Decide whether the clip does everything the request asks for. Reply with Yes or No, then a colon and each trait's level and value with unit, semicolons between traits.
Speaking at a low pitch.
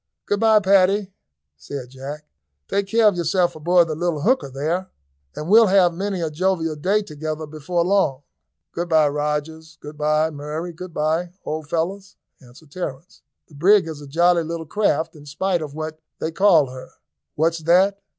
No: medium, 165 Hz